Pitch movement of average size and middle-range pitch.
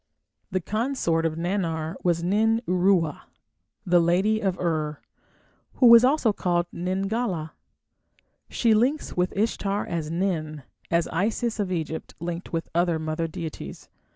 Yes: average, 4.0 semitones; medium, 180 Hz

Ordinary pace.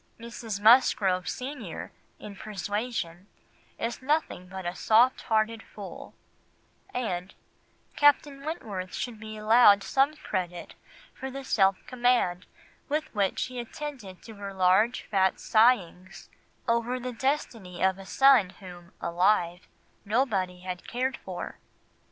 No: slow, 120 wpm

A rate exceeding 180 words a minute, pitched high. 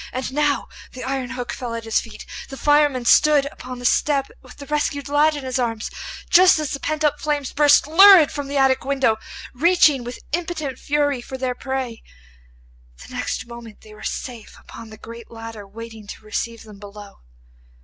Yes: average, 190 wpm; very high, 260 Hz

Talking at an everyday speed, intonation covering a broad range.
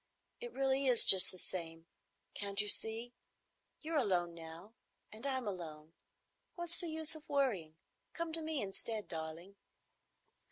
Yes: average, 145 wpm; wide, 8.3 semitones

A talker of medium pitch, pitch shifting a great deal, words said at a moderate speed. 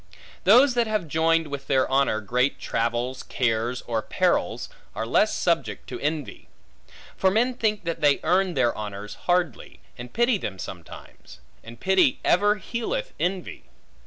Yes: medium, 160 Hz; wide, 8.6 semitones; average, 150 wpm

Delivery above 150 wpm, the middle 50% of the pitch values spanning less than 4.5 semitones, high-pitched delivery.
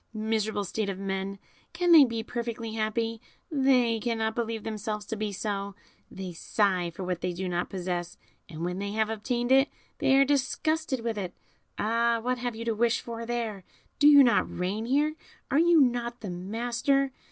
Yes: average, 185 wpm; average, 3.4 semitones; high, 225 Hz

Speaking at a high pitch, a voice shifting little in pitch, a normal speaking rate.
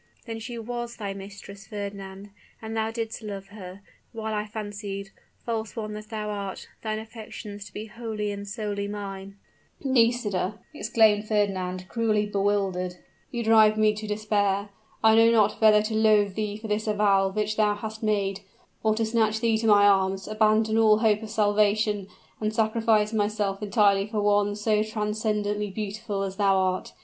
Yes: high, 210 Hz; narrow, 1.4 semitones; average, 165 wpm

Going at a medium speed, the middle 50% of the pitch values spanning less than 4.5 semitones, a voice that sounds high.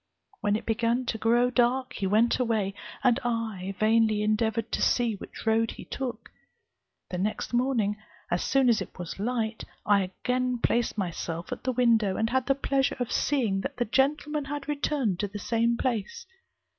Yes: average, 180 wpm; average, 3.2 semitones; high, 230 Hz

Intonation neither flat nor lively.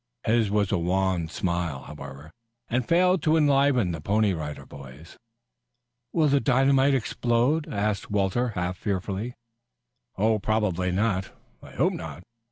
No: wide, 5.8 semitones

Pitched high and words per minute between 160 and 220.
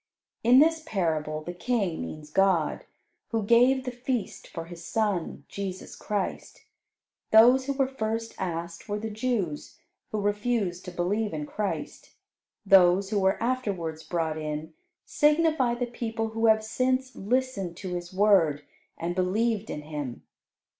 No: high, 205 Hz; average, 145 wpm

